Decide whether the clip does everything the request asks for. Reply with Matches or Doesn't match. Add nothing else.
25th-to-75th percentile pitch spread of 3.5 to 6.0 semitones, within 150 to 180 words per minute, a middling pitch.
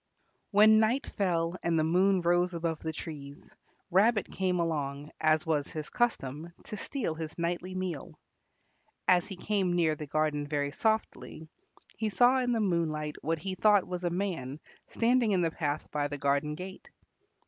Matches